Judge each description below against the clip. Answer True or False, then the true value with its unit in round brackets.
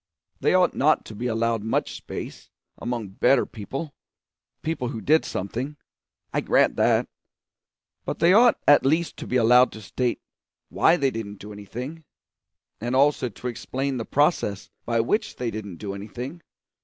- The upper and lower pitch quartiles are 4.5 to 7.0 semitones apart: True (4.8 semitones)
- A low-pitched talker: True (125 Hz)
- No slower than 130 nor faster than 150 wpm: False (160 wpm)